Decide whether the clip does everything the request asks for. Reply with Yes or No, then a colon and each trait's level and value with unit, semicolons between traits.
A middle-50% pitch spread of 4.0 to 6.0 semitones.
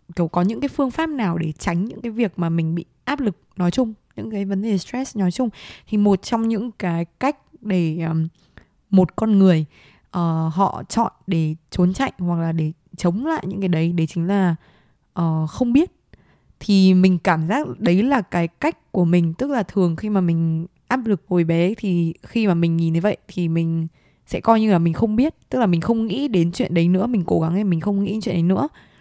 Yes: average, 4.8 semitones